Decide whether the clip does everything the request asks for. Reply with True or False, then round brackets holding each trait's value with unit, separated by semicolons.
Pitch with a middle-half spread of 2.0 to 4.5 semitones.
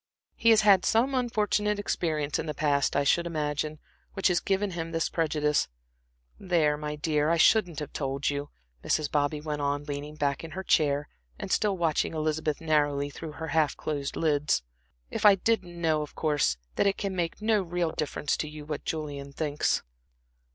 True (3.1 semitones)